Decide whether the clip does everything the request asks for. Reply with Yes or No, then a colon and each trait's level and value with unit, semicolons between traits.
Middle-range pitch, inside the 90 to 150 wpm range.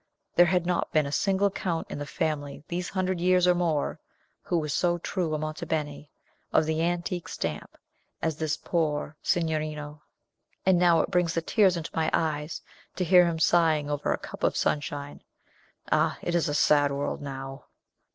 No: medium, 160 Hz; average, 180 wpm